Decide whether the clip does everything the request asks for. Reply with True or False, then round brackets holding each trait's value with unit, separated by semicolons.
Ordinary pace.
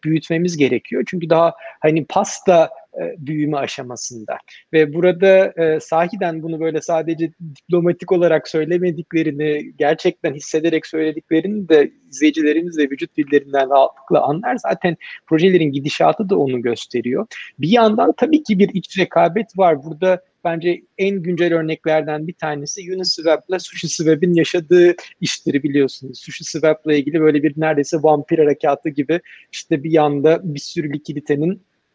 True (130 wpm)